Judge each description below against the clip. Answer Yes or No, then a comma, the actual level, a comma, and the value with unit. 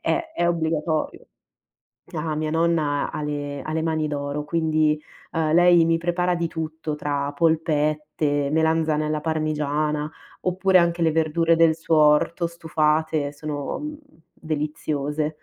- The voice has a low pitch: No, medium, 155 Hz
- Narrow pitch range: Yes, narrow, 1.6 semitones